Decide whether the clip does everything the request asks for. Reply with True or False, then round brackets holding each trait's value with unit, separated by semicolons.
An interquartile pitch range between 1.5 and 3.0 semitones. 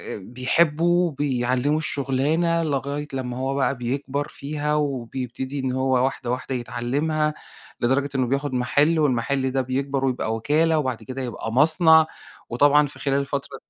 True (2.6 semitones)